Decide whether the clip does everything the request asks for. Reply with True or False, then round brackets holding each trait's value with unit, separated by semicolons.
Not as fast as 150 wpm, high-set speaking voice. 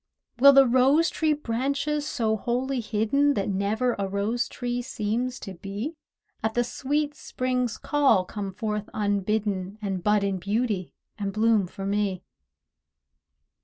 True (140 wpm; 220 Hz)